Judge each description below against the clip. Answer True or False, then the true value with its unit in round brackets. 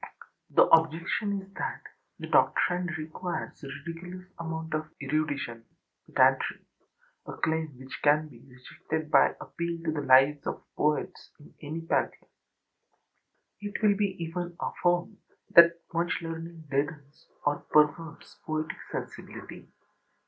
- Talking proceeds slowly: True (125 wpm)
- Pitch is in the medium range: True (160 Hz)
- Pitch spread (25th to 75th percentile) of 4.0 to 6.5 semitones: False (2.4 semitones)